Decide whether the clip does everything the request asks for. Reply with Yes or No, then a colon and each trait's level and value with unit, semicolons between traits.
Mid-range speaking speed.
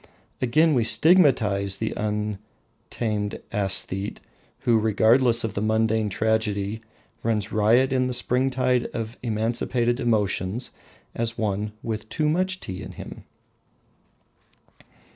No: slow, 110 wpm